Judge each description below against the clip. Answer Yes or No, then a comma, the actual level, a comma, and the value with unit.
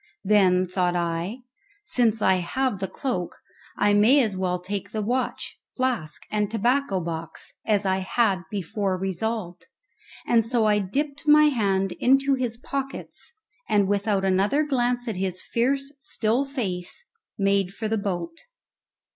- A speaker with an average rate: Yes, average, 145 wpm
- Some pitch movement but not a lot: Yes, average, 4.8 semitones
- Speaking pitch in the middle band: No, high, 210 Hz